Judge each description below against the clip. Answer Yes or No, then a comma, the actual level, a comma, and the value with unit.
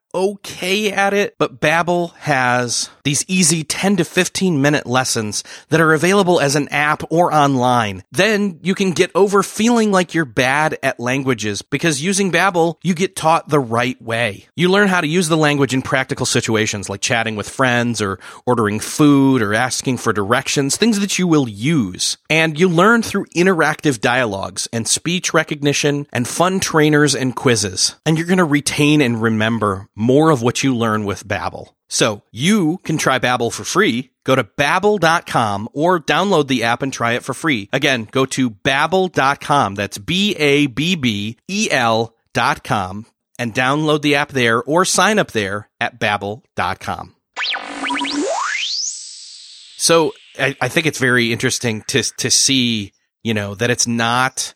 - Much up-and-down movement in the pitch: Yes, wide, 6.4 semitones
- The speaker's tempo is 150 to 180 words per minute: Yes, average, 165 wpm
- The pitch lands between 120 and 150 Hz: Yes, medium, 140 Hz